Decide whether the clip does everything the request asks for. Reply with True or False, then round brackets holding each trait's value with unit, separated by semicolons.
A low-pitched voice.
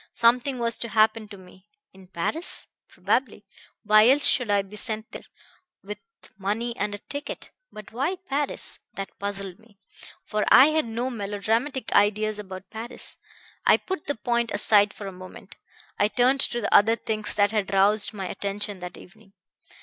False (215 Hz)